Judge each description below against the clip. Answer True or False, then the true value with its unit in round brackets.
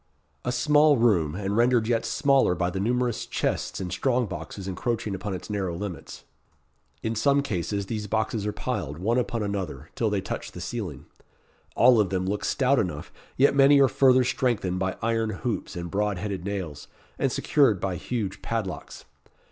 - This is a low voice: True (105 Hz)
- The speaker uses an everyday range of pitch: True (4.7 semitones)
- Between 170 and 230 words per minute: True (175 wpm)